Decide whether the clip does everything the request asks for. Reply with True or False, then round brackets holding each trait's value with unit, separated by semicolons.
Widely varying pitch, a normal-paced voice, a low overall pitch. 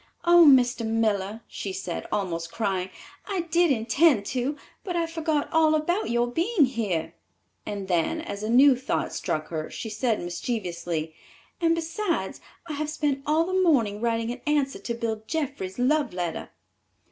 False (7.5 semitones; 160 wpm; 245 Hz)